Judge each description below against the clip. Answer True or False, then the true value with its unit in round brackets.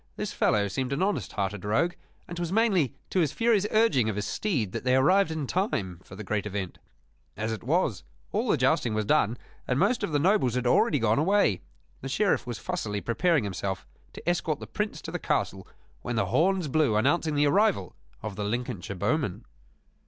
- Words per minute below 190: False (200 wpm)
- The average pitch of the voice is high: False (130 Hz)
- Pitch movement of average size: False (8.7 semitones)